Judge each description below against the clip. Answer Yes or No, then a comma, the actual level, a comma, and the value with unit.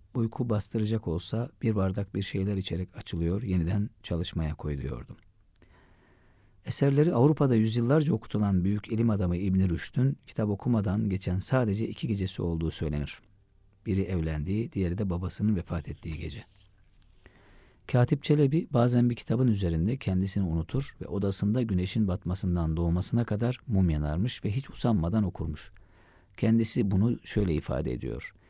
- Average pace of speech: Yes, average, 130 wpm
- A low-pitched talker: Yes, low, 100 Hz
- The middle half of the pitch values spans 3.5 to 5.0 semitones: Yes, average, 4.1 semitones